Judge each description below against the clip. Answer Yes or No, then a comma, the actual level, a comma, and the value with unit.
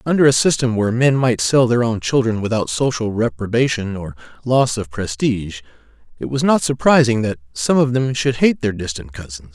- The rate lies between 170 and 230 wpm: Yes, average, 190 wpm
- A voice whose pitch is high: No, low, 115 Hz